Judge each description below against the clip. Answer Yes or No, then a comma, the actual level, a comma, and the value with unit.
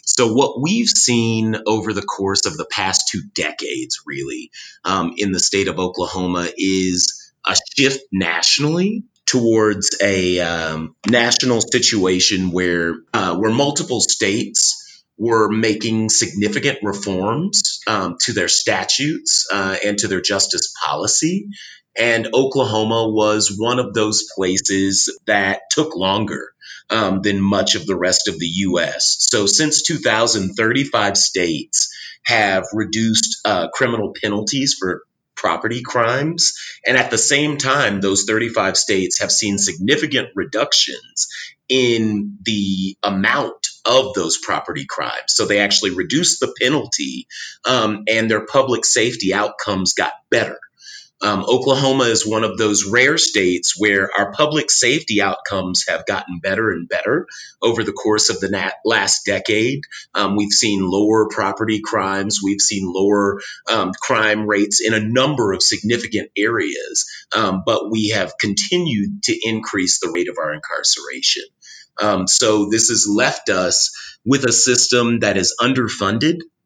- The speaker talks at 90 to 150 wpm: Yes, average, 140 wpm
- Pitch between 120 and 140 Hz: No, low, 110 Hz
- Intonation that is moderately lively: Yes, average, 4.0 semitones